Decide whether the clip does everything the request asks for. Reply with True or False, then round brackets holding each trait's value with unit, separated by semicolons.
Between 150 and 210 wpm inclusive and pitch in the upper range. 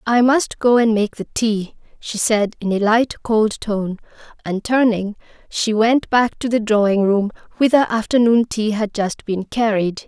True (180 wpm; 220 Hz)